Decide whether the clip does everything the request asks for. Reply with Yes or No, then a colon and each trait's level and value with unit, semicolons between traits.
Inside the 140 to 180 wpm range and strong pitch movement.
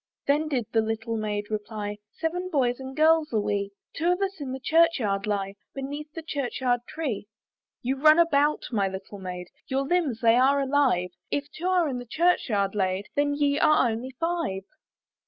No: average, 190 wpm; wide, 6.4 semitones